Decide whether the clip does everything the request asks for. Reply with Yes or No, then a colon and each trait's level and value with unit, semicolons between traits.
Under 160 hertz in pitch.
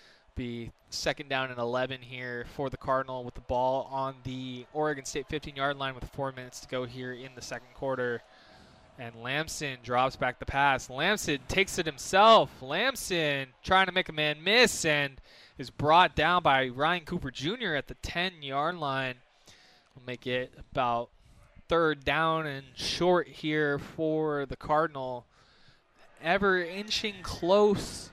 Yes: low, 135 Hz